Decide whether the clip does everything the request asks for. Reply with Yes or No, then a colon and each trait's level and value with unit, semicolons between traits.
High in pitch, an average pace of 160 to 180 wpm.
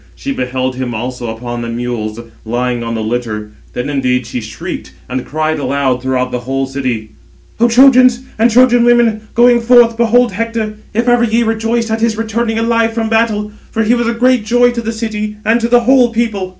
No: high, 220 Hz; average, 200 wpm